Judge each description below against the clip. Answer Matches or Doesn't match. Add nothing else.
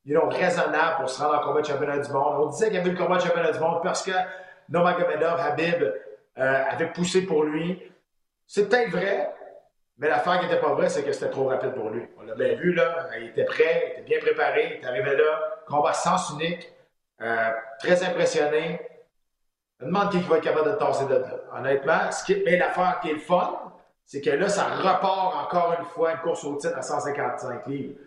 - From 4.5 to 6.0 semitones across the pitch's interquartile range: Matches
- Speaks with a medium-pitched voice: Matches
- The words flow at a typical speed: Doesn't match